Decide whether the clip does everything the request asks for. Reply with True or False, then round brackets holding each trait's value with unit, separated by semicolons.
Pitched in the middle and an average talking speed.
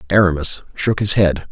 False (90 Hz; 160 wpm)